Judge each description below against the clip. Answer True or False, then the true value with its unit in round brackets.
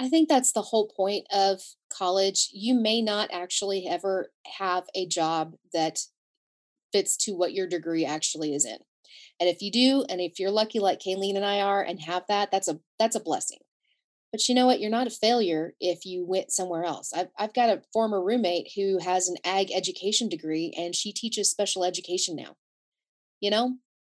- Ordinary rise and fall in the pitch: True (3.4 semitones)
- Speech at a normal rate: True (195 wpm)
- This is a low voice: False (195 Hz)